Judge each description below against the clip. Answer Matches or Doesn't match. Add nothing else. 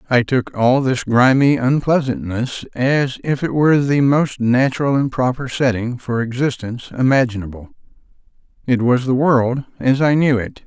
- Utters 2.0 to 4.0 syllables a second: Doesn't match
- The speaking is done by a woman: Doesn't match